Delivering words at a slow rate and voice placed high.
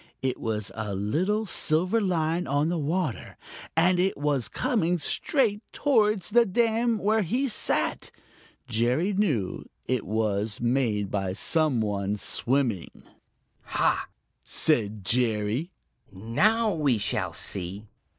No: slow, 120 wpm; medium, 145 Hz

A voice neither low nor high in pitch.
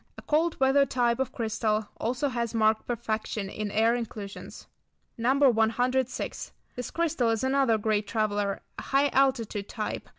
No: high, 235 Hz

